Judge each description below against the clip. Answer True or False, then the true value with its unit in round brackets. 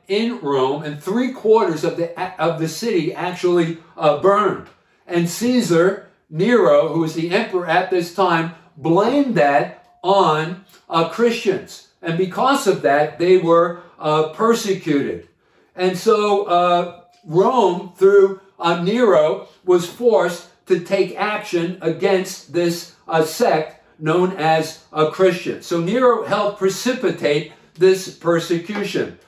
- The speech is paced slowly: True (130 wpm)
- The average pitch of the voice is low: False (180 Hz)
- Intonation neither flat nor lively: True (3.0 semitones)